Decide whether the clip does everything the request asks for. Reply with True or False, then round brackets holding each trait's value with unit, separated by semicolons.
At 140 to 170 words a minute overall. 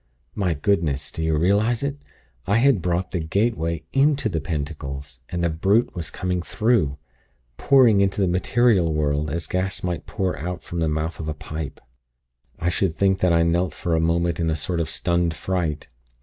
False (190 wpm)